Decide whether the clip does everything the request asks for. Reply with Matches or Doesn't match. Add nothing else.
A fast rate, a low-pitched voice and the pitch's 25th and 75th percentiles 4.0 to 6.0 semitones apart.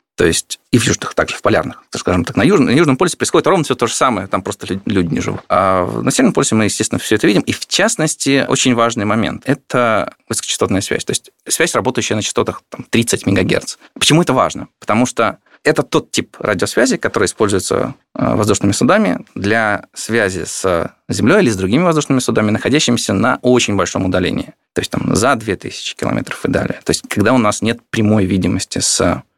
Matches